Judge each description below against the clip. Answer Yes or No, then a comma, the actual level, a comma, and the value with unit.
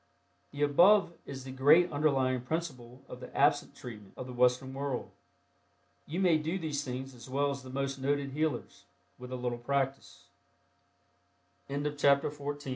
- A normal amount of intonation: No, narrow, 2.3 semitones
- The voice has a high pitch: No, medium, 140 Hz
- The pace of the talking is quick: No, average, 155 wpm